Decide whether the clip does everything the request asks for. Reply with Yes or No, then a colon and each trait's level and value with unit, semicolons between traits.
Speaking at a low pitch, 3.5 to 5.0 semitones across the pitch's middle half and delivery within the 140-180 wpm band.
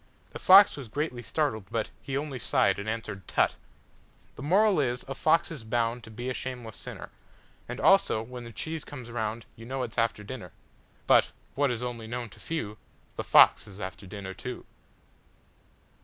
Yes: low, 120 Hz; average, 3.8 semitones; average, 160 wpm